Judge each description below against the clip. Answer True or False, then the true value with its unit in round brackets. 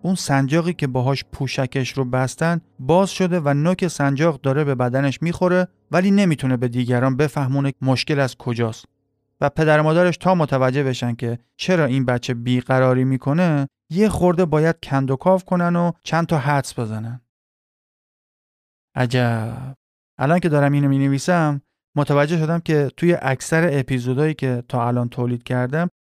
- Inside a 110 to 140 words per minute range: False (150 wpm)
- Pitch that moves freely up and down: False (4.3 semitones)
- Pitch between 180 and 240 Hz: False (140 Hz)